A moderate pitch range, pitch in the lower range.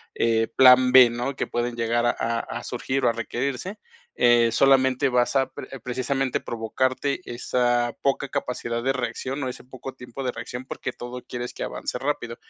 No: narrow, 1.8 semitones; low, 125 Hz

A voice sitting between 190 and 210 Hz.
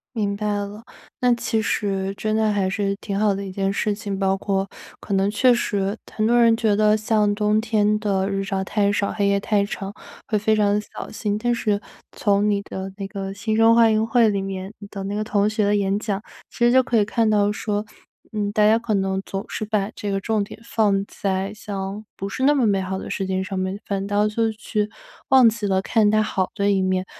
Yes: high, 205 Hz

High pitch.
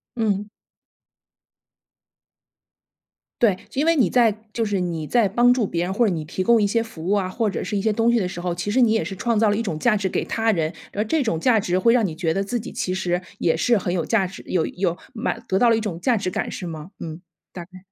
Yes: high, 200 Hz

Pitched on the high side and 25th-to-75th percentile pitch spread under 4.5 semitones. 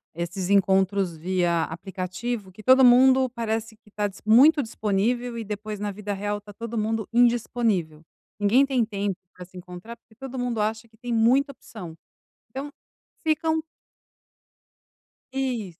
Yes: high, 220 Hz; average, 4.0 semitones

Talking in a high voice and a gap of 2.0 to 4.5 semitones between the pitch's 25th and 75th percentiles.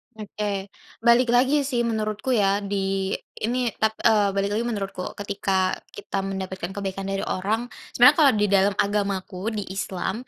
Yes: high, 205 Hz; narrow, 2.4 semitones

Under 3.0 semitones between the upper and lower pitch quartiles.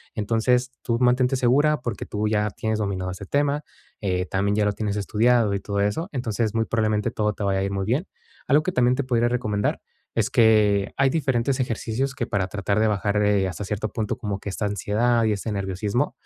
No: average, 3.3 semitones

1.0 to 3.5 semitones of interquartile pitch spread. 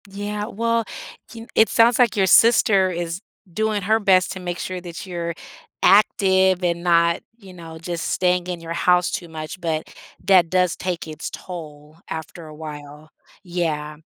Yes: average, 2.7 semitones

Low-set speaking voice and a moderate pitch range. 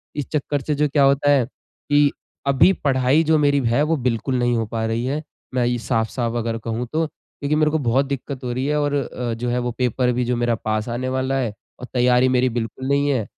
Yes: low, 130 Hz; average, 3.0 semitones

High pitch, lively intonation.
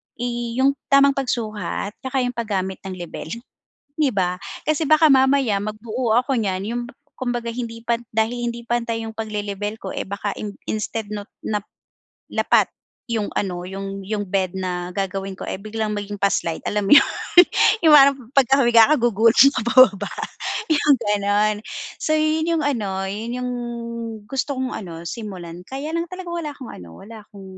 No: high, 225 Hz; average, 4.5 semitones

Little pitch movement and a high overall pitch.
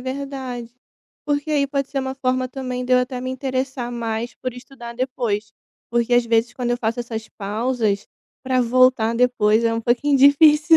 Yes: narrow, 2.2 semitones; very high, 250 Hz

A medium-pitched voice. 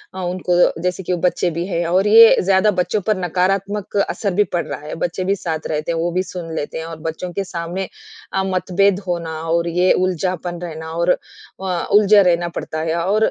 Yes: medium, 180 Hz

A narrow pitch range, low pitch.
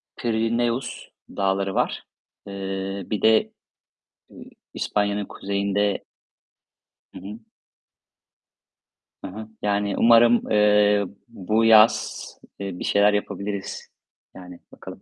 Yes: narrow, 1.9 semitones; low, 105 Hz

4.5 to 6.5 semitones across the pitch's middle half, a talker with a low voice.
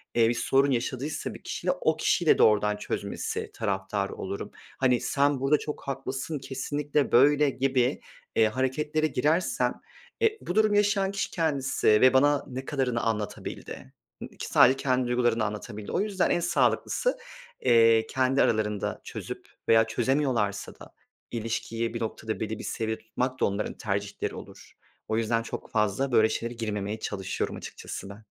No: average, 4.0 semitones; low, 125 Hz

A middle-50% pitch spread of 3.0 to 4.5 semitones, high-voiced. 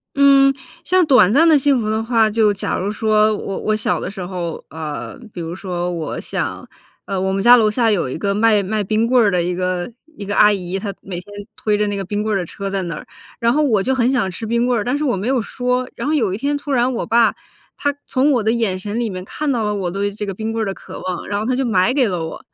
Yes: average, 4.1 semitones; high, 215 Hz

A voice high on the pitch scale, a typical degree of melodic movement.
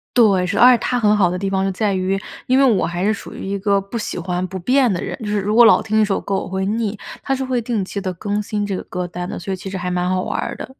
Yes: high, 200 Hz; average, 3.0 semitones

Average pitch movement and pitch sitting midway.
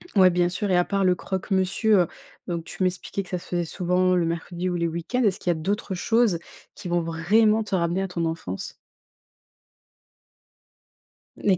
No: narrow, 2.2 semitones; medium, 180 Hz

